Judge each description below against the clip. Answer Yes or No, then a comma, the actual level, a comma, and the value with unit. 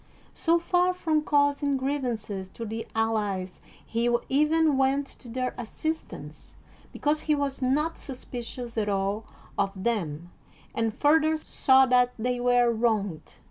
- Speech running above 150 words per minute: No, average, 140 wpm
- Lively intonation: No, average, 4.7 semitones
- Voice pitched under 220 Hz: No, very high, 250 Hz